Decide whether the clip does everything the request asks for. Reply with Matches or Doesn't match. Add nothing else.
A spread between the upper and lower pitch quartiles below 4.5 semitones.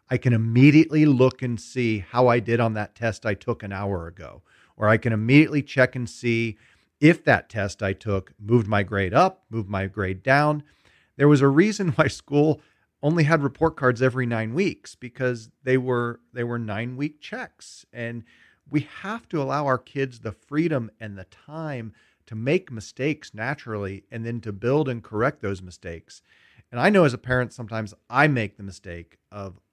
Doesn't match